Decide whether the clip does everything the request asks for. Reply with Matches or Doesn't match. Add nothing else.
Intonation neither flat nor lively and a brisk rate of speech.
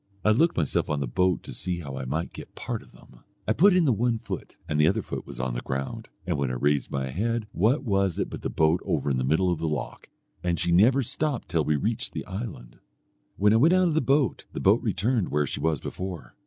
Doesn't match